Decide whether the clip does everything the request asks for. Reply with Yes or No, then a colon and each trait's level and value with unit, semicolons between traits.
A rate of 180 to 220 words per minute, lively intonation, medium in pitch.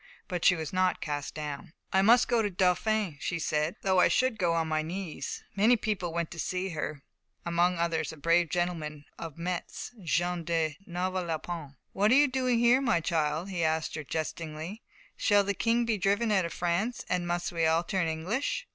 No: average, 200 wpm; average, 3.7 semitones; medium, 175 Hz